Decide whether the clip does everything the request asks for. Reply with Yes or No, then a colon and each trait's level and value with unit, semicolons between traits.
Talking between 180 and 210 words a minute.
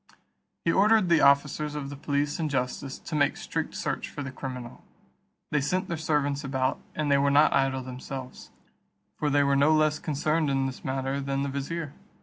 Yes: average, 190 wpm